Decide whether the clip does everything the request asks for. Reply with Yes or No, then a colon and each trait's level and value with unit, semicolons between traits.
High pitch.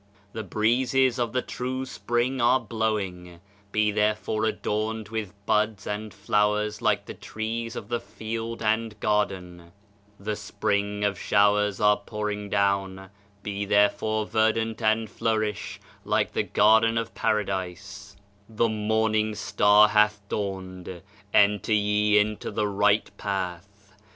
No: low, 105 Hz